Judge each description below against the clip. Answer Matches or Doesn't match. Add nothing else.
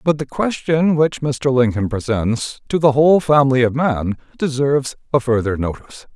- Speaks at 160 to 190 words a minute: Matches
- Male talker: Matches